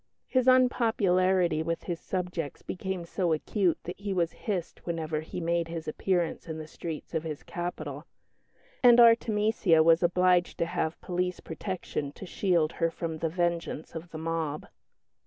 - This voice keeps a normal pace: Yes, average, 155 wpm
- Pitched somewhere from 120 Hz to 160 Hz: No, medium, 170 Hz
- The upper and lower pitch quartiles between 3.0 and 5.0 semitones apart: No, narrow, 2.4 semitones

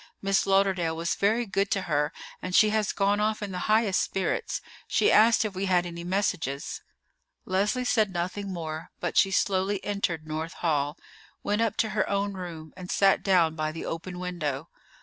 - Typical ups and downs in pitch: Yes, average, 3.2 semitones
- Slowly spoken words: No, average, 185 wpm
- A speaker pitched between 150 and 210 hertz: Yes, high, 190 Hz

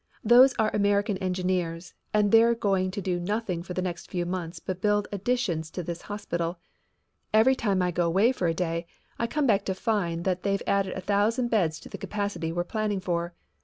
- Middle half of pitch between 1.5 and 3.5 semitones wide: Yes, average, 3.2 semitones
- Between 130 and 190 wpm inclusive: No, average, 200 wpm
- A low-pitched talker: No, high, 190 Hz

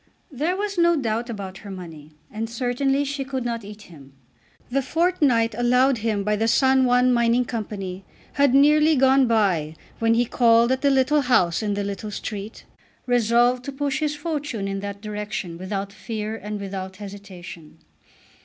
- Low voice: No, high, 230 Hz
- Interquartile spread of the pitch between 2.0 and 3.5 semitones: No, average, 4.8 semitones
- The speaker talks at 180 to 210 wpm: No, average, 165 wpm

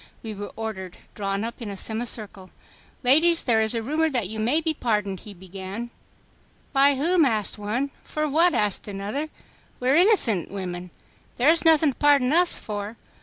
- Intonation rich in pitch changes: Yes, wide, 6.2 semitones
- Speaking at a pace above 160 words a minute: Yes, average, 180 wpm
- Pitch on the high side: Yes, high, 230 Hz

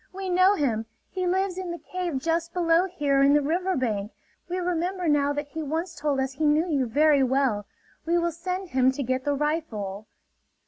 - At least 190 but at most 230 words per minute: Yes, average, 200 wpm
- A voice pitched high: Yes, very high, 310 Hz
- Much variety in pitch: No, average, 4.6 semitones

